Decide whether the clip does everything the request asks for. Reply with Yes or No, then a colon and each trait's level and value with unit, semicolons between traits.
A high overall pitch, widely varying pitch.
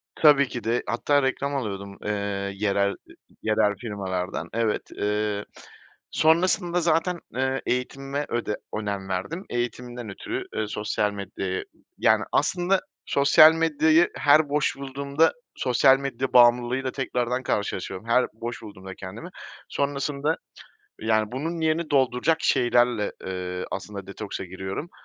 No: low, 120 Hz; wide, 5.7 semitones